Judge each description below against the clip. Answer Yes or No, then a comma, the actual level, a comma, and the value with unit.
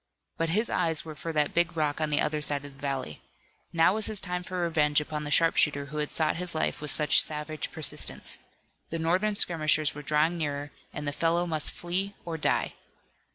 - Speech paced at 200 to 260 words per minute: Yes, fast, 205 wpm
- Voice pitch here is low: No, medium, 155 Hz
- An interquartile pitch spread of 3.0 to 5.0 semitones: No, narrow, 2.5 semitones